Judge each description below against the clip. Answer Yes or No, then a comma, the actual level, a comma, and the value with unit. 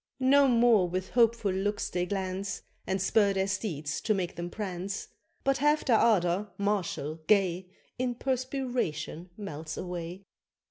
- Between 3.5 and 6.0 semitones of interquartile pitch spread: Yes, average, 4.3 semitones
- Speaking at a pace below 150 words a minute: Yes, average, 140 wpm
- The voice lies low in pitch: No, high, 195 Hz